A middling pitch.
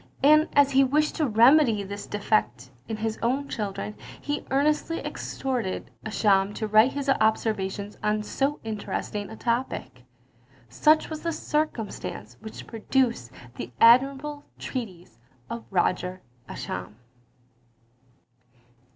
No: high, 225 Hz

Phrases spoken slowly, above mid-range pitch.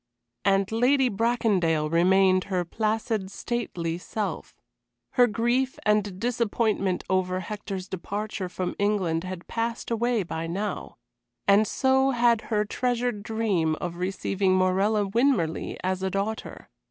Yes: slow, 125 wpm; high, 205 Hz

